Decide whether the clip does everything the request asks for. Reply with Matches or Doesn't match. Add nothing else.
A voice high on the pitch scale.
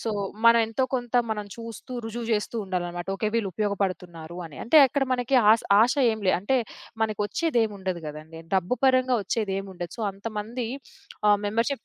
Matches